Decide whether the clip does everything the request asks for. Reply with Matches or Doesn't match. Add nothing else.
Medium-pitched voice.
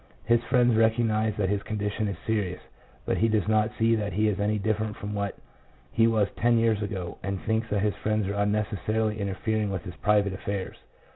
Doesn't match